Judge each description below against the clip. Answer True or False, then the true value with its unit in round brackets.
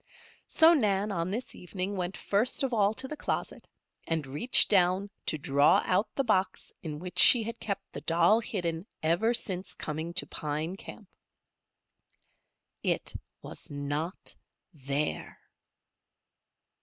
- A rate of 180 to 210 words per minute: False (135 wpm)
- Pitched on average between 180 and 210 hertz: True (185 Hz)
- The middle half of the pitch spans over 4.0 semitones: True (4.8 semitones)